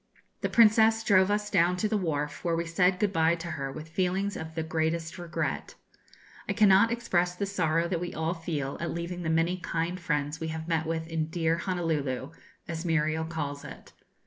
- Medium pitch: Yes, medium, 170 Hz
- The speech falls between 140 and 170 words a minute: No, average, 200 wpm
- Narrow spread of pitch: Yes, narrow, 2.3 semitones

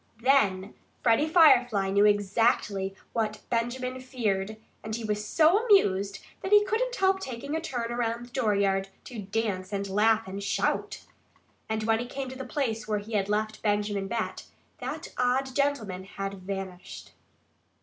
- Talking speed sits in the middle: Yes, average, 160 wpm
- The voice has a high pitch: Yes, high, 220 Hz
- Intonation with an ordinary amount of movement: Yes, average, 4.3 semitones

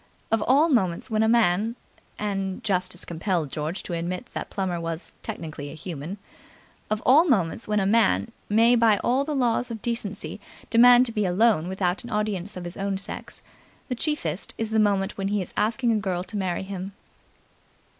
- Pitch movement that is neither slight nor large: Yes, average, 4.1 semitones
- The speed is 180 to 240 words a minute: Yes, average, 185 wpm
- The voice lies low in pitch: No, high, 205 Hz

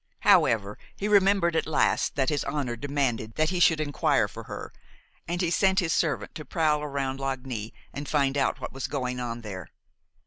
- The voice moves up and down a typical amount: Yes, average, 4.3 semitones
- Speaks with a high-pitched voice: No, medium, 145 Hz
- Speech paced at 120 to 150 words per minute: No, average, 185 wpm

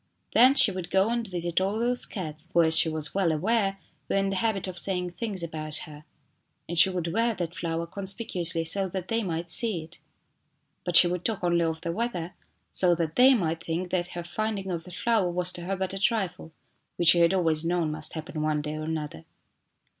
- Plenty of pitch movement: No, average, 3.0 semitones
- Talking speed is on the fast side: Yes, fast, 220 wpm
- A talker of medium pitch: Yes, medium, 175 Hz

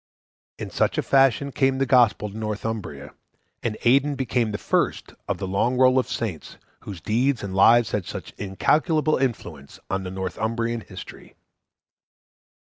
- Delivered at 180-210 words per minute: No, average, 145 wpm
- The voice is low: Yes, low, 115 Hz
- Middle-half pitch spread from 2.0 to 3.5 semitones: No, average, 4.5 semitones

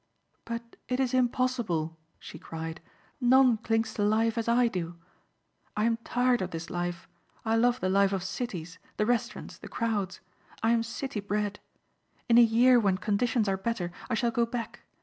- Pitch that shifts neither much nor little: Yes, average, 3.9 semitones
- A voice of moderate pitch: No, high, 225 Hz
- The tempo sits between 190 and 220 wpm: No, average, 175 wpm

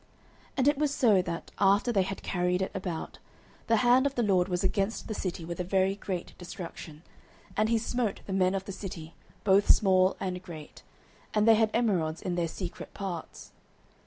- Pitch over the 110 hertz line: Yes, high, 190 Hz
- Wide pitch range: No, average, 3.2 semitones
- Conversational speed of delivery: Yes, average, 195 wpm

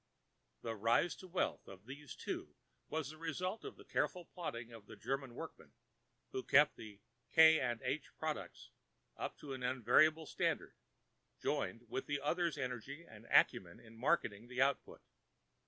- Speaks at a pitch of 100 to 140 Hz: Yes, low, 135 Hz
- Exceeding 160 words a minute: No, average, 155 wpm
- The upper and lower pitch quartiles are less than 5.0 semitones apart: No, average, 5.3 semitones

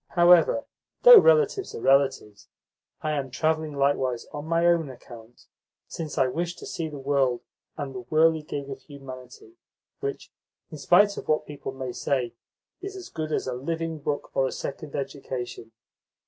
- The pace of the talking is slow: No, average, 160 wpm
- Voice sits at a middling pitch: Yes, medium, 145 Hz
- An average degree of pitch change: Yes, average, 3.9 semitones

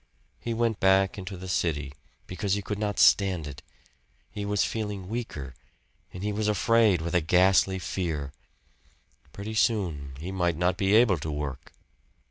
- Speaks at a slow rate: No, average, 160 wpm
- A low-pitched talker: Yes, very low, 95 Hz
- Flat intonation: No, average, 3.7 semitones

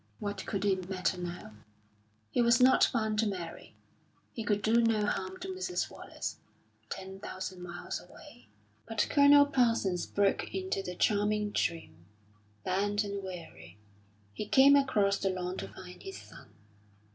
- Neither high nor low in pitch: No, high, 200 Hz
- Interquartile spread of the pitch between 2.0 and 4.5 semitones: Yes, average, 3.7 semitones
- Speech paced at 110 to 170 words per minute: Yes, average, 150 wpm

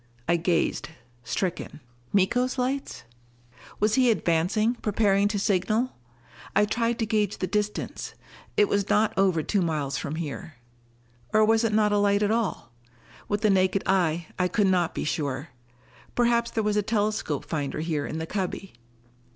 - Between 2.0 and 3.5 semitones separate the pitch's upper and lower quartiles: No, average, 4.2 semitones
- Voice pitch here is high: Yes, high, 200 Hz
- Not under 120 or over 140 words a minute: No, average, 160 wpm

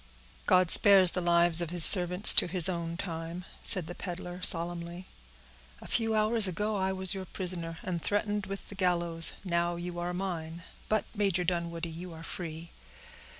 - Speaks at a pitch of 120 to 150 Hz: No, medium, 175 Hz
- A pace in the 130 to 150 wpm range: No, average, 170 wpm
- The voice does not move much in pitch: Yes, narrow, 2.0 semitones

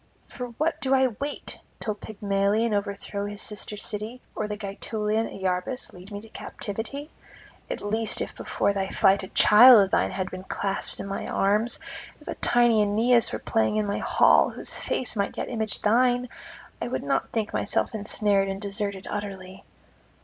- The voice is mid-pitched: No, high, 210 Hz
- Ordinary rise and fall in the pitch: No, narrow, 2.3 semitones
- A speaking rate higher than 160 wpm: Yes, average, 170 wpm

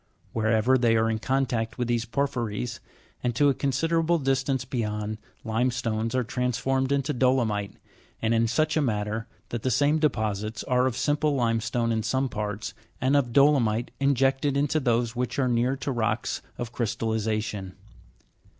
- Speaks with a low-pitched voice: Yes, low, 120 Hz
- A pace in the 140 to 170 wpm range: Yes, average, 160 wpm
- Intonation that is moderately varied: Yes, average, 3.1 semitones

